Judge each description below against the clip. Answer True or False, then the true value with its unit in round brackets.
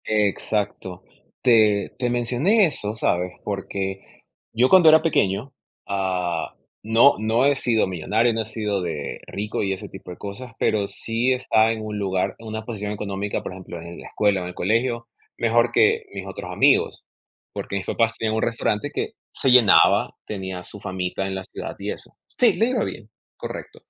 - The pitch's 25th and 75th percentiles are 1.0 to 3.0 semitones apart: False (3.4 semitones)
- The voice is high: False (105 Hz)